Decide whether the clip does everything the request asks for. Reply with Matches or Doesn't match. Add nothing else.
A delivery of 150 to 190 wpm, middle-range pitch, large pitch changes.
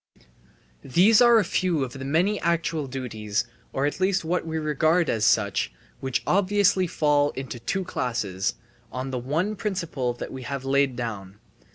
Matches